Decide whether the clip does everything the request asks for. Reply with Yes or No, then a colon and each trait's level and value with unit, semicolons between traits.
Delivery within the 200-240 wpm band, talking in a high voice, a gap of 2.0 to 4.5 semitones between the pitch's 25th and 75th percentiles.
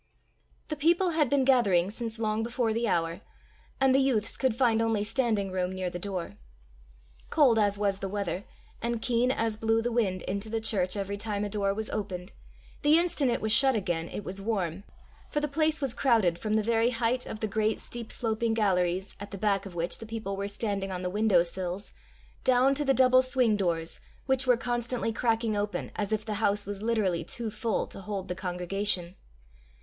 Yes: fast, 205 wpm; high, 215 Hz; average, 3.4 semitones